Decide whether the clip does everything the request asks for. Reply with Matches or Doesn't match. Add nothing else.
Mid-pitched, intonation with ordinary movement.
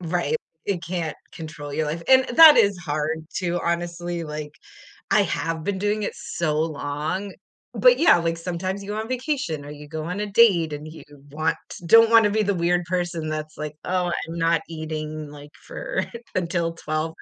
Matches